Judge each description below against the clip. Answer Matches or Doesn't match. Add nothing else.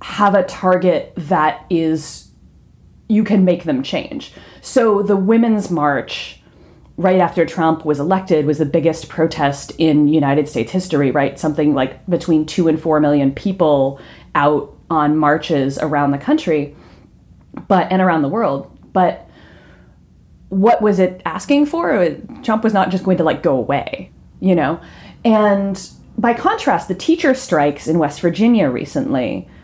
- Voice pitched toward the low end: Doesn't match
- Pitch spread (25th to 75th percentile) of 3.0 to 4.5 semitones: Doesn't match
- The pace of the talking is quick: Doesn't match